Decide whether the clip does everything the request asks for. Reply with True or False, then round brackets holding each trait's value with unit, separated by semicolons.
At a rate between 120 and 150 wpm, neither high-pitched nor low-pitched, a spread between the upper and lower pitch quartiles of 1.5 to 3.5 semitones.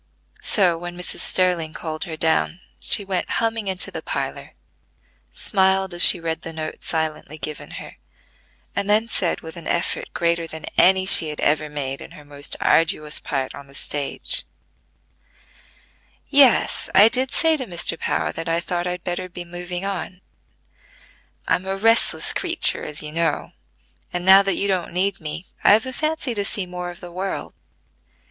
False (170 wpm; 175 Hz; 3.2 semitones)